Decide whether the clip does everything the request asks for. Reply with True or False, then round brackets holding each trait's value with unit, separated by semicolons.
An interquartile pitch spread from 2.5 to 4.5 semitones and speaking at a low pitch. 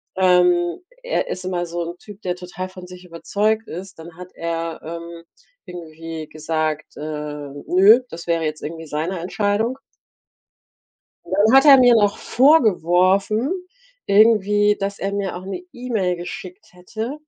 False (3.8 semitones; 180 Hz)